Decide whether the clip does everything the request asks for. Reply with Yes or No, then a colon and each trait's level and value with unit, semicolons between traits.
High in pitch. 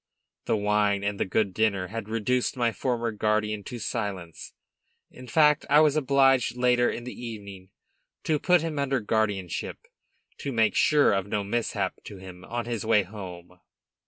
No: low, 110 Hz